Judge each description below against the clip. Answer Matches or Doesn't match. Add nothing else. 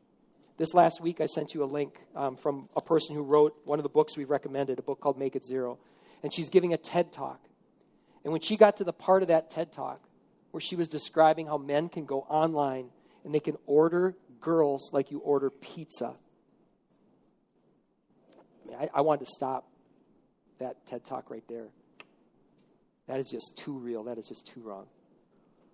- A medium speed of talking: Matches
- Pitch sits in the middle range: Matches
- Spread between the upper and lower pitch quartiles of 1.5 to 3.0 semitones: Matches